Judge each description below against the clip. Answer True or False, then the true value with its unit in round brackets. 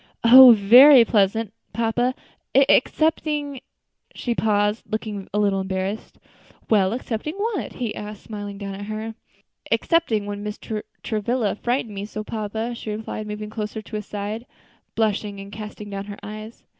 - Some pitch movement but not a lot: False (2.3 semitones)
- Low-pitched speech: False (215 Hz)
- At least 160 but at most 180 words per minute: False (150 wpm)